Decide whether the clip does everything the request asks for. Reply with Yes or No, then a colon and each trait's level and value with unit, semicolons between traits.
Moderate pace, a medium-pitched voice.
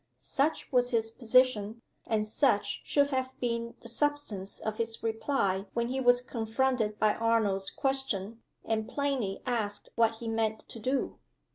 No: average, 150 wpm; high, 230 Hz